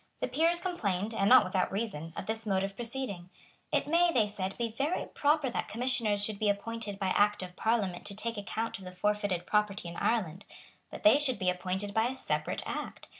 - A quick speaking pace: Yes, fast, 210 wpm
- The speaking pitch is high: Yes, high, 210 Hz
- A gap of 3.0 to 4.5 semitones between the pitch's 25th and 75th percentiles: Yes, average, 3.7 semitones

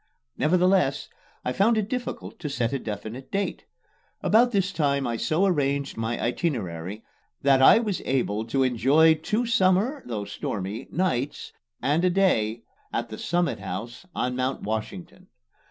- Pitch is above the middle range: No, medium, 140 Hz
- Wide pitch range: Yes, wide, 7.9 semitones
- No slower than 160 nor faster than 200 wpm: No, average, 150 wpm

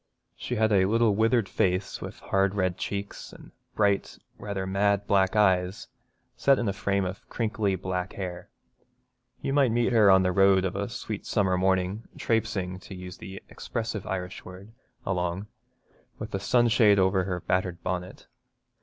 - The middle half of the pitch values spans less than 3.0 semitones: Yes, narrow, 2.4 semitones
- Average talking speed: Yes, average, 165 wpm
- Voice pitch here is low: Yes, very low, 95 Hz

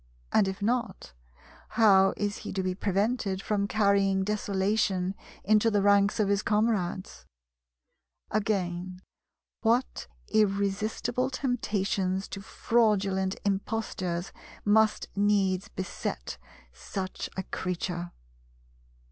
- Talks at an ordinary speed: No, slow, 95 wpm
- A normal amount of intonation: No, narrow, 2.1 semitones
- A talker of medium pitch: No, high, 200 Hz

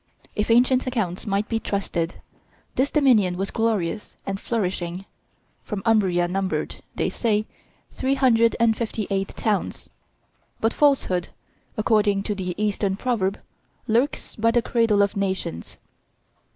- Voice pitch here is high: Yes, high, 210 Hz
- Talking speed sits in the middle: No, slow, 130 wpm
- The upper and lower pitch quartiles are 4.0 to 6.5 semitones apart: No, average, 3.1 semitones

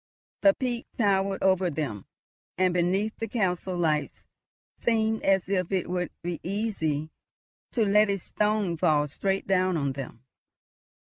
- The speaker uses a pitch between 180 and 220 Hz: Yes, medium, 185 Hz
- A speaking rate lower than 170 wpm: Yes, average, 140 wpm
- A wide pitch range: No, average, 3.7 semitones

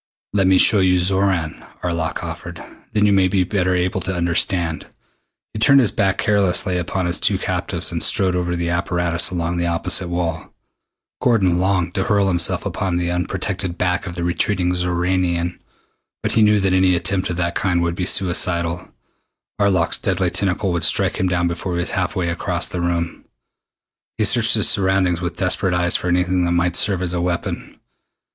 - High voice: No, very low, 90 Hz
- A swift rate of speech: No, average, 185 wpm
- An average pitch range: No, narrow, 1.5 semitones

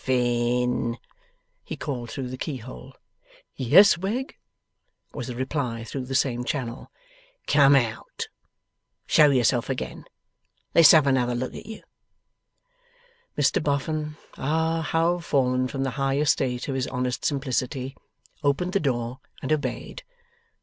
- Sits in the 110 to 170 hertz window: Yes, low, 135 Hz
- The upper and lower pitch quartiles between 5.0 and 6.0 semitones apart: No, average, 3.2 semitones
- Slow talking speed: Yes, slow, 130 wpm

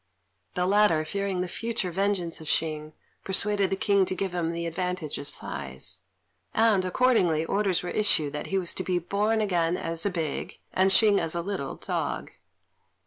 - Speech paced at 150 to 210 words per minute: Yes, average, 180 wpm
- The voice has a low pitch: No, medium, 185 Hz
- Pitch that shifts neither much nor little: Yes, average, 3.2 semitones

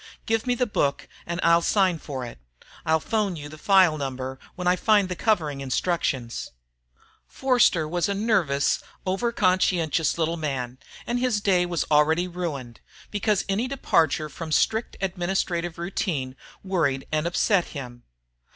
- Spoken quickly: No, average, 150 wpm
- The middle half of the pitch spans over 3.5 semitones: Yes, average, 4.8 semitones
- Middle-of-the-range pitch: Yes, medium, 170 Hz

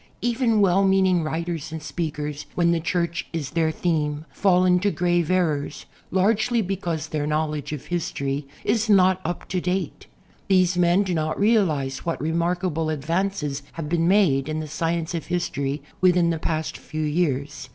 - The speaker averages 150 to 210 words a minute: Yes, average, 165 wpm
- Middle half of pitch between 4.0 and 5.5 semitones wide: No, average, 3.1 semitones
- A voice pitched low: No, medium, 170 Hz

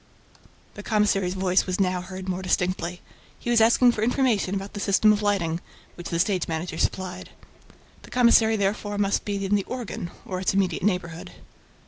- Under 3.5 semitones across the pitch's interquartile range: Yes, narrow, 2.4 semitones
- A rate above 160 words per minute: Yes, average, 175 wpm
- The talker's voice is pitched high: Yes, high, 195 Hz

